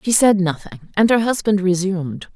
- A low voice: No, high, 190 Hz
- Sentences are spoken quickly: No, average, 180 wpm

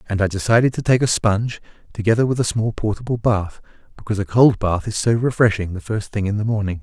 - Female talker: No, male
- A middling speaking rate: No, fast, 230 wpm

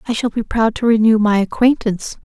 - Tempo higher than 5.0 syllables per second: Yes, 5.8 syllables/s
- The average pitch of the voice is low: No, high, 220 Hz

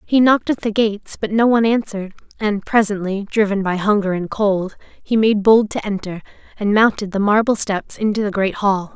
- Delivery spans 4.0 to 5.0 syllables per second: No, 5.4 syllables/s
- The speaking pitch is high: Yes, high, 205 Hz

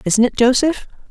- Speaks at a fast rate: No, average, 165 wpm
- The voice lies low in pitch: No, very high, 250 Hz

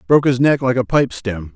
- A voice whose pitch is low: Yes, low, 125 Hz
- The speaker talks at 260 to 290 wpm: Yes, fast, 270 wpm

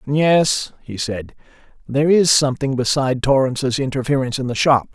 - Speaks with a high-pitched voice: No, low, 135 Hz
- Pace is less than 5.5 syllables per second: No, 5.6 syllables/s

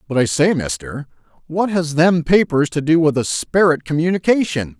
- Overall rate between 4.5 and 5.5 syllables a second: Yes, 5.0 syllables/s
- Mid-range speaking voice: Yes, medium, 155 Hz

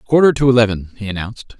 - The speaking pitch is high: No, low, 115 Hz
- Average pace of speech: Yes, average, 190 wpm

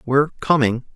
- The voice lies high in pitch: No, low, 135 Hz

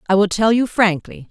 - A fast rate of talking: Yes, fast, 230 wpm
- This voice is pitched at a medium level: No, high, 205 Hz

